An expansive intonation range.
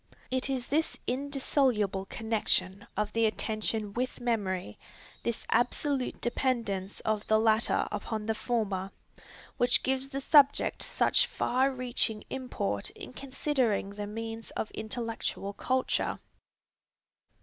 No: average, 3.6 semitones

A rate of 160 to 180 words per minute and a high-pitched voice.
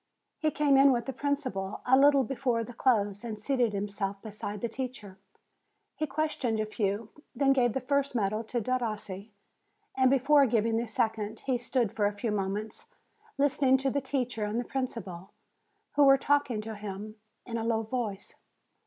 Yes: average, 175 wpm; high, 235 Hz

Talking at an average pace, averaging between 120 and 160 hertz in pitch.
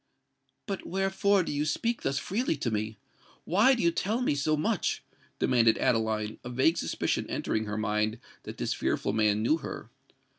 Yes: average, 175 wpm; medium, 140 Hz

